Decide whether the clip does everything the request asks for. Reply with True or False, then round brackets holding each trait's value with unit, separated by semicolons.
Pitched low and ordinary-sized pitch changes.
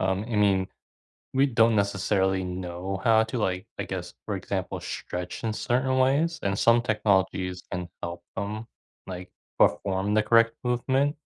True (105 Hz; 3.8 semitones)